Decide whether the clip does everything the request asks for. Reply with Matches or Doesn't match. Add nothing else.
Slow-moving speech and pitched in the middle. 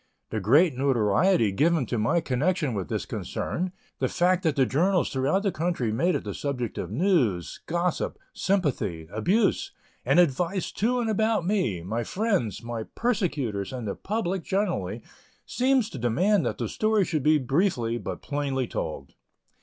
Doesn't match